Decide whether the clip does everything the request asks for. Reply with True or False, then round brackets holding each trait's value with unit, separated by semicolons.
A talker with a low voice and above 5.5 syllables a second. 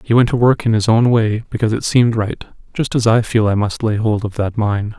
True (110 Hz; 5.7 syllables/s)